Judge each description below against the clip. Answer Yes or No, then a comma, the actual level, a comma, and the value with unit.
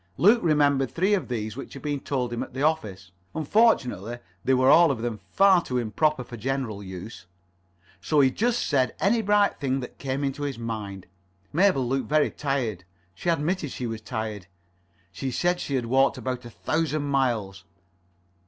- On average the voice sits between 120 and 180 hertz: Yes, low, 135 Hz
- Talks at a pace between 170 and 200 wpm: Yes, average, 180 wpm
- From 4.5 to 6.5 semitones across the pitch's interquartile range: Yes, average, 4.9 semitones